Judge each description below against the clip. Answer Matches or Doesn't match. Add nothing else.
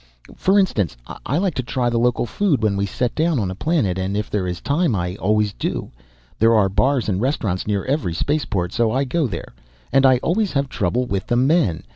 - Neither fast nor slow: Doesn't match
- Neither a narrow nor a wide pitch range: Doesn't match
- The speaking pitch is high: Doesn't match